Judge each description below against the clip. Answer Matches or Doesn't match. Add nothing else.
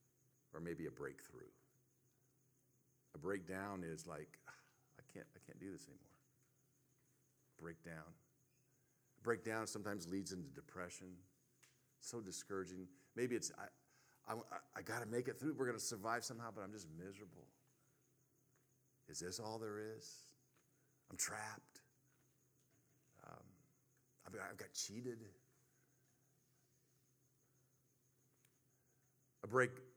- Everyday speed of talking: Doesn't match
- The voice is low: Matches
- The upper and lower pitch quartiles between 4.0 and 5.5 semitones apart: Doesn't match